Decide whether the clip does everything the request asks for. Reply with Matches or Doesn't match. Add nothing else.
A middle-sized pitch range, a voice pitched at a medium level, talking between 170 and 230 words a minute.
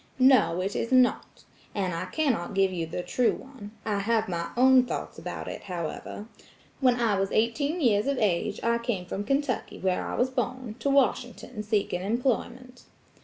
Doesn't match